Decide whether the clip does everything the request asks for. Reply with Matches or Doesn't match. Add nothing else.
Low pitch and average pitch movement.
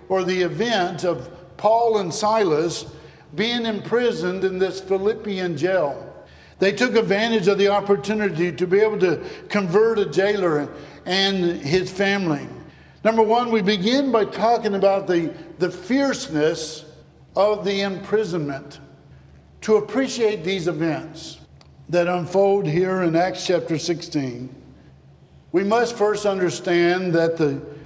Doesn't match